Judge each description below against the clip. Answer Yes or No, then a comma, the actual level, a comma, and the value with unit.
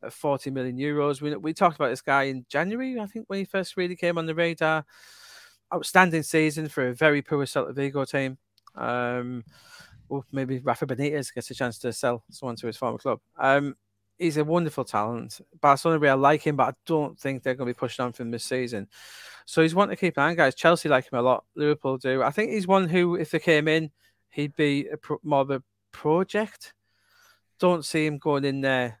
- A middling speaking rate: No, fast, 225 wpm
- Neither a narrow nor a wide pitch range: Yes, average, 4.2 semitones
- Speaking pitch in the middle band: Yes, medium, 145 Hz